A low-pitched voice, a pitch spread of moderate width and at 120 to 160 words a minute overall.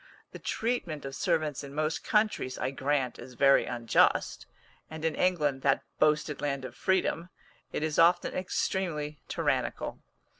No: medium, 150 Hz; average, 4.0 semitones; average, 145 wpm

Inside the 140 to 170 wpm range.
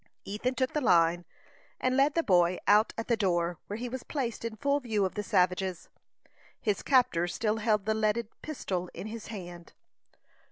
No: average, 185 wpm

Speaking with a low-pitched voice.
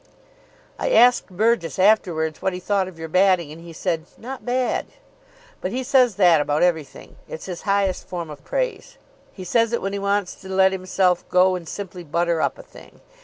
No: medium, 185 Hz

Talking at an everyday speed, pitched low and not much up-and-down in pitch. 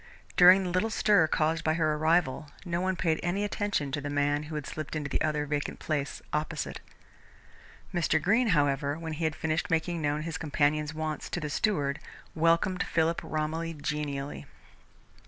No: average, 175 wpm; medium, 155 Hz; narrow, 2.3 semitones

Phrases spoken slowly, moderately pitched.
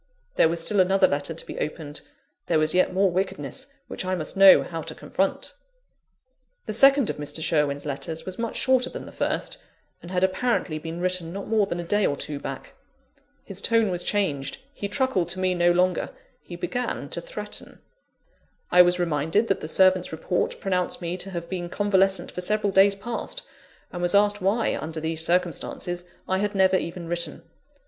No: average, 190 wpm; medium, 180 Hz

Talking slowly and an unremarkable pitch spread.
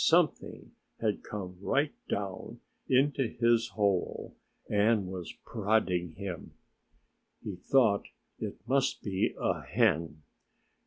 Yes: slow, 105 wpm; average, 4.1 semitones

